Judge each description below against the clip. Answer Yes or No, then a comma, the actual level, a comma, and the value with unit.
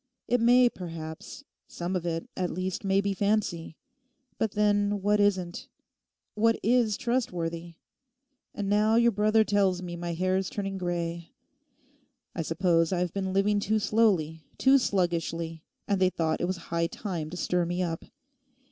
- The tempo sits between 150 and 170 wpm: Yes, average, 155 wpm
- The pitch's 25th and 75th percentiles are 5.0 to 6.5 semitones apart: No, average, 3.5 semitones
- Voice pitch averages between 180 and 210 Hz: Yes, medium, 185 Hz